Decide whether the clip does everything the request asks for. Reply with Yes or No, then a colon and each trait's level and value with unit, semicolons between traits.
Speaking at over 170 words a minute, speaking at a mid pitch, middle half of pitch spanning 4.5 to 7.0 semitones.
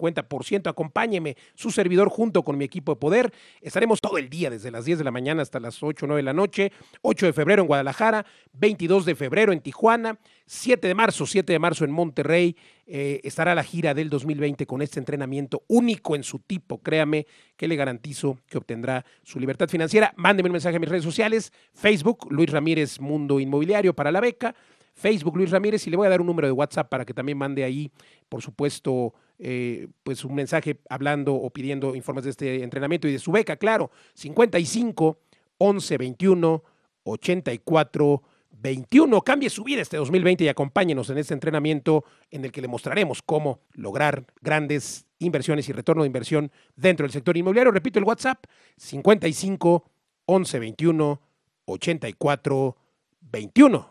Yes: average, 185 wpm; medium, 155 Hz; average, 5.0 semitones